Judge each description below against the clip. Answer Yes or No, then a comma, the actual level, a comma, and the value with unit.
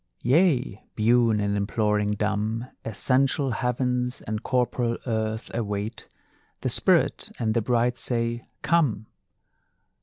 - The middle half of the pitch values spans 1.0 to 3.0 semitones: Yes, narrow, 2.5 semitones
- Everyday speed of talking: No, slow, 110 wpm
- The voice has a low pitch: Yes, low, 115 Hz